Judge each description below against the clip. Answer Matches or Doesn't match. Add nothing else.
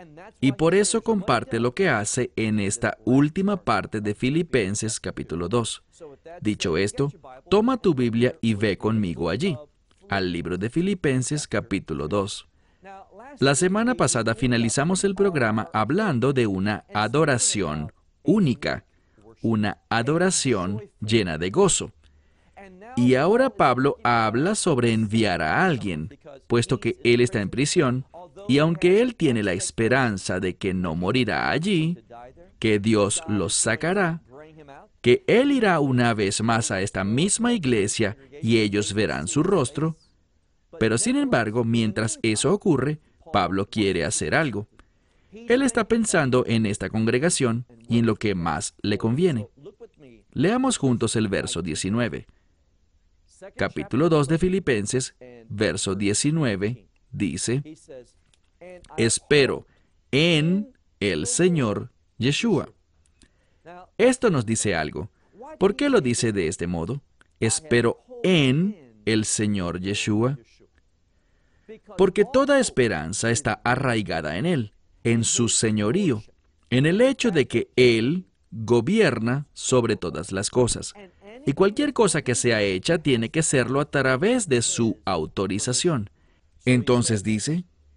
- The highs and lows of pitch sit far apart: Matches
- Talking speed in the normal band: Doesn't match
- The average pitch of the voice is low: Matches